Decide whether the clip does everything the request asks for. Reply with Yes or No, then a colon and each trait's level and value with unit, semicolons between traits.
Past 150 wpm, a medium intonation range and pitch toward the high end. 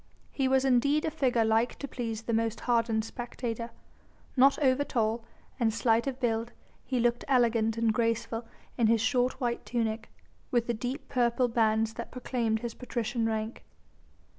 No: average, 165 wpm; narrow, 1.8 semitones; high, 235 Hz